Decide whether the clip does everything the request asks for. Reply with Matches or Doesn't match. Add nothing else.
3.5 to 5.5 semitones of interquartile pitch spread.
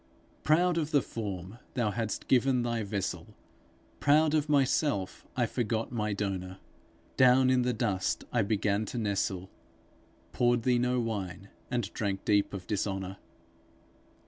Matches